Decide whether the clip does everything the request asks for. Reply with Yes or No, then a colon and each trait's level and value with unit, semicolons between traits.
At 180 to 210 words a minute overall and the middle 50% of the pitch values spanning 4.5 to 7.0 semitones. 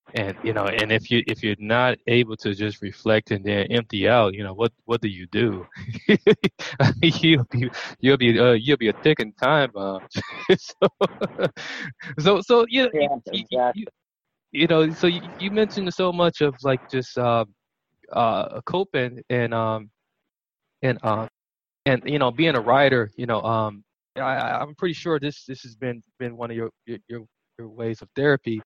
Yes: average, 185 wpm; average, 5.0 semitones